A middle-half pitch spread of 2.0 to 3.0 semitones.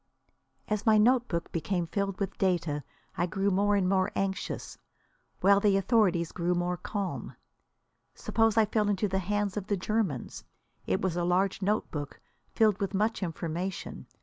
Yes: average, 2.7 semitones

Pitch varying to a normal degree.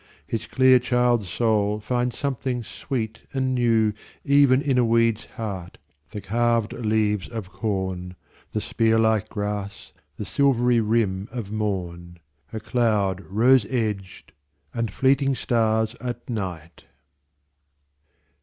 Yes: average, 3.1 semitones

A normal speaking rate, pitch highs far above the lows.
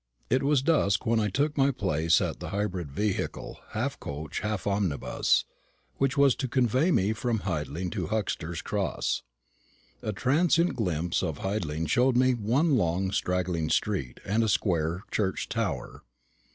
Yes: average, 150 wpm; wide, 6.4 semitones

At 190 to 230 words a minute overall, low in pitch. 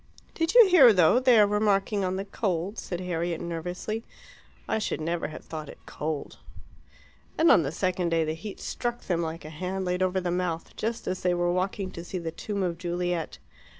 No: fast, 205 wpm; medium, 180 Hz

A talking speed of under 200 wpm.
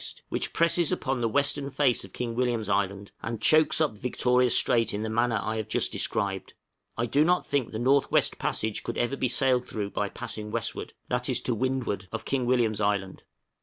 No: fast, 205 wpm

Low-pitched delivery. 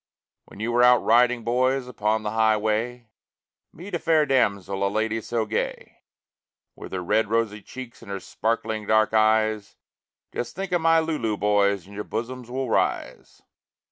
Yes: low, 110 Hz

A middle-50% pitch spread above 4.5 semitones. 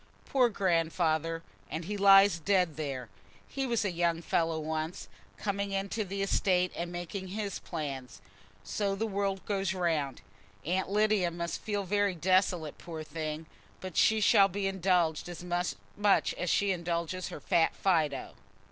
No: average, 3.2 semitones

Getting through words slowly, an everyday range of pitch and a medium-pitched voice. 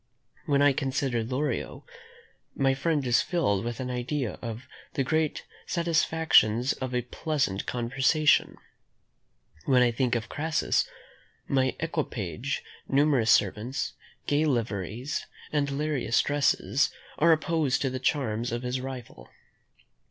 No: slow, 120 wpm; average, 3.6 semitones; low, 130 Hz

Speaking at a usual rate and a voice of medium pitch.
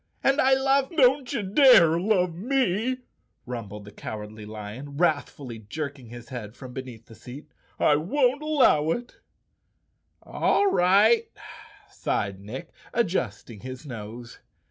No: slow, 130 wpm; medium, 150 Hz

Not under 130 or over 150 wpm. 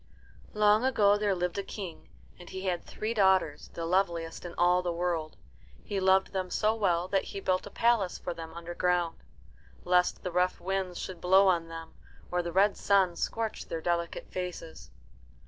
No: average, 180 wpm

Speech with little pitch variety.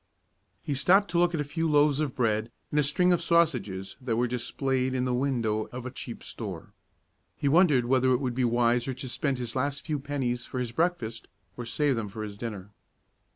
No: average, 3.7 semitones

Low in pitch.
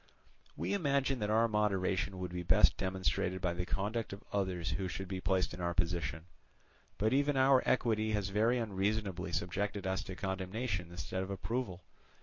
Yes: very low, 95 Hz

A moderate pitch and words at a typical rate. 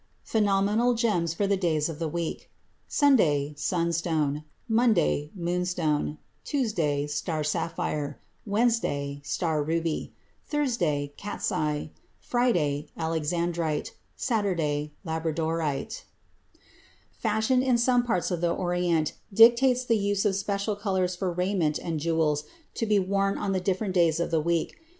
No: medium, 175 Hz; slow, 125 wpm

